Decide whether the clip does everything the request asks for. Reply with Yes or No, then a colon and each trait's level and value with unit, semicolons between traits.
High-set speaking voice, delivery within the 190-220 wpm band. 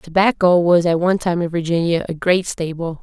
No: medium, 170 Hz; average, 200 wpm